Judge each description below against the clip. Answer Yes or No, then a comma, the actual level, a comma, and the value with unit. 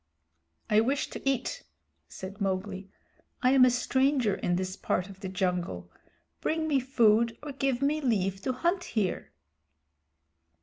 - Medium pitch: No, high, 225 Hz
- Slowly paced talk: No, average, 145 wpm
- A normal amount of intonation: No, wide, 6.0 semitones